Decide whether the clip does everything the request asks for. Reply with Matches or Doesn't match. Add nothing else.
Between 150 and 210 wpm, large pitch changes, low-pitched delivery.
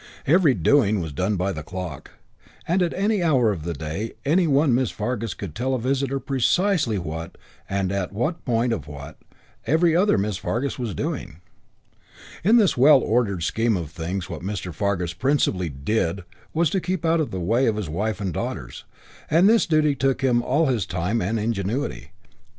Matches